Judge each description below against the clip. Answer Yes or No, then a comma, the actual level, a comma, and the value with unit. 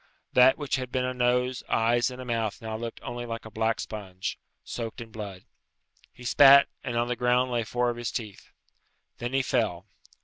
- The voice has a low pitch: Yes, low, 120 Hz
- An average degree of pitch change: No, narrow, 2.0 semitones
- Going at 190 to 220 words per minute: Yes, average, 200 wpm